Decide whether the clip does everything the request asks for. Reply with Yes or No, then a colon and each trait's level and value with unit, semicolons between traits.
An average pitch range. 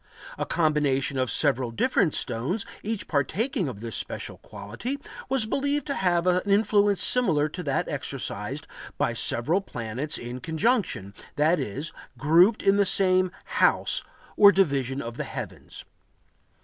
No: wide, 7.3 semitones